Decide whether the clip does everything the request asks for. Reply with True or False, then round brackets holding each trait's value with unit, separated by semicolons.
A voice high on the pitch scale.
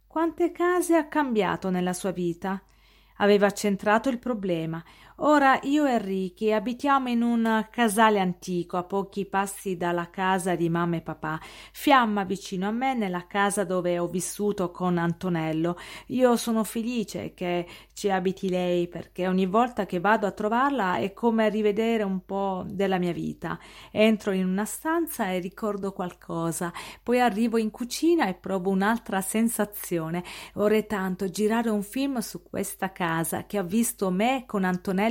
True (200 Hz)